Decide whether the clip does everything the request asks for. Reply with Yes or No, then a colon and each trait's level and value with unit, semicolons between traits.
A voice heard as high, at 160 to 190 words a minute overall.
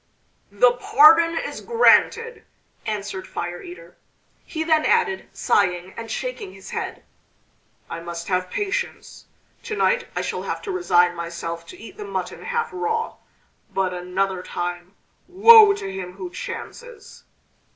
No: high, 220 Hz; average, 140 wpm